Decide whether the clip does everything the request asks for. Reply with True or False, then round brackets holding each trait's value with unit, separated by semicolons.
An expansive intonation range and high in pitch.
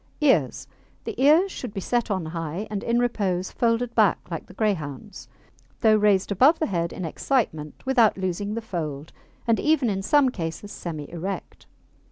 True (5.7 semitones; 205 Hz)